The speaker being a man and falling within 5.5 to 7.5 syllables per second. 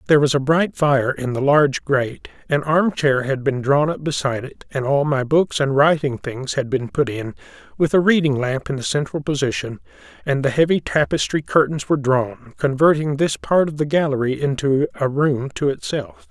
No: male; 5.2 syllables/s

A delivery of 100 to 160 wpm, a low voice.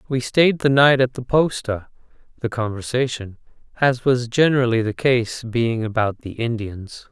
Yes: average, 150 wpm; low, 120 Hz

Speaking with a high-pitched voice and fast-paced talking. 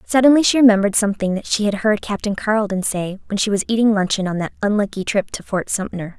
Yes: high, 205 Hz; fast, 225 wpm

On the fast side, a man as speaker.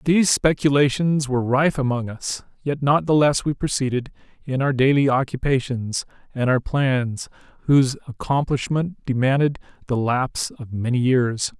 No: average, 140 wpm; male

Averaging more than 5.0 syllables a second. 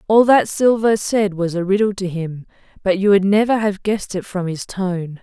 No: 4.9 syllables/s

